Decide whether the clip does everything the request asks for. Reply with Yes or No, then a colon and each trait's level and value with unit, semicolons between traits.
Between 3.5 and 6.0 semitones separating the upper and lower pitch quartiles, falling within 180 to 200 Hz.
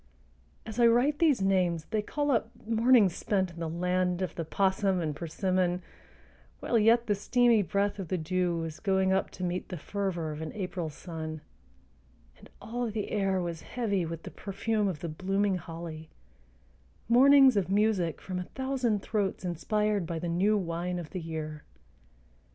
Yes: average, 3.9 semitones; high, 190 Hz